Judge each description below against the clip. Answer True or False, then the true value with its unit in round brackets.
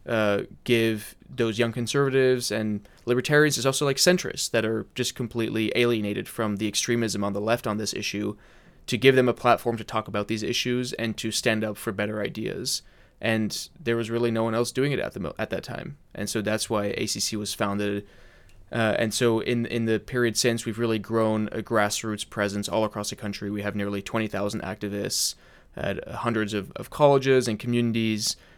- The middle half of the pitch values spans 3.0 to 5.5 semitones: False (2.4 semitones)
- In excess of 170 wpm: True (200 wpm)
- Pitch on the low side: True (110 Hz)